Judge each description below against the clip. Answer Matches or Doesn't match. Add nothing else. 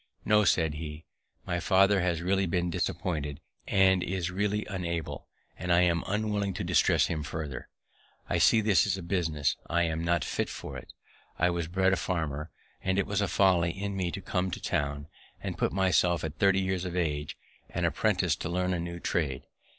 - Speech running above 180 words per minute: Matches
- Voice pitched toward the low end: Matches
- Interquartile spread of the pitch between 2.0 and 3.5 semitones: Matches